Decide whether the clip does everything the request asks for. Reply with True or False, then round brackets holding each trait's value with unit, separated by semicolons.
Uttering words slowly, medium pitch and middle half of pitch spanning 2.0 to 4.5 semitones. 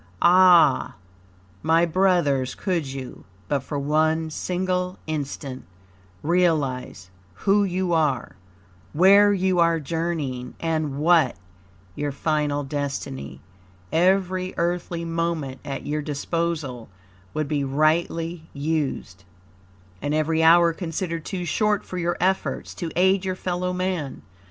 True (115 wpm; 165 Hz; 3.7 semitones)